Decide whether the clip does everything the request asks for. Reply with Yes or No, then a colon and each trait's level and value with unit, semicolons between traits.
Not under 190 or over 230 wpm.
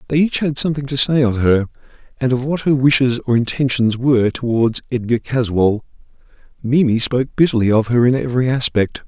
No: average, 180 wpm